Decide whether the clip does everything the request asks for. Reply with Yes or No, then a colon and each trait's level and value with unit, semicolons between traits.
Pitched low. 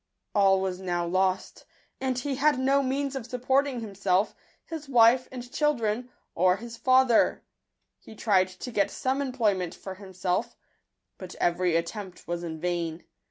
No: high, 210 Hz